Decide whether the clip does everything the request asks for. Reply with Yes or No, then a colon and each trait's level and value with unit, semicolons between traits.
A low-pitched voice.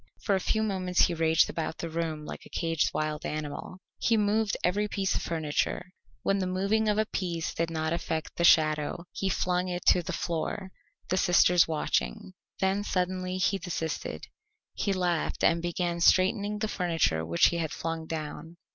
No: medium, 175 Hz